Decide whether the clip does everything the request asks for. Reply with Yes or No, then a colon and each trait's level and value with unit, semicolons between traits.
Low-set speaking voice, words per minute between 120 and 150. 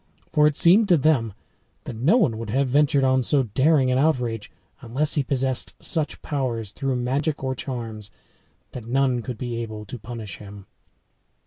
No: low, 130 Hz; average, 175 wpm